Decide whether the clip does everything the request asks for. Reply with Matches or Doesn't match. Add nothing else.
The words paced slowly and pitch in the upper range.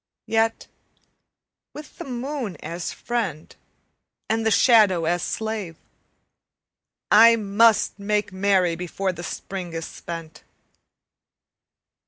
Matches